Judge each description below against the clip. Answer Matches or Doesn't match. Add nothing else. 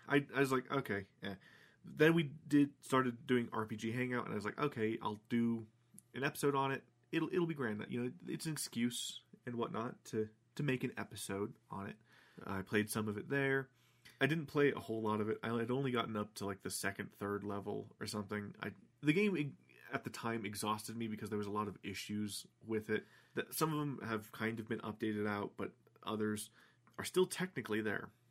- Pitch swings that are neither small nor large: Matches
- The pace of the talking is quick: Matches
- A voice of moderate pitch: Doesn't match